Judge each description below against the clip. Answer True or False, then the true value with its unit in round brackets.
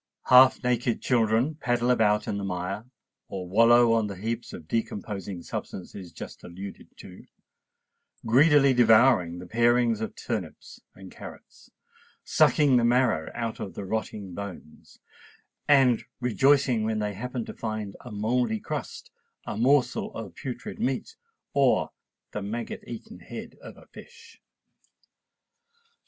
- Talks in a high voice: False (115 Hz)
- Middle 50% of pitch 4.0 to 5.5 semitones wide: False (3.5 semitones)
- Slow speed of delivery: True (130 wpm)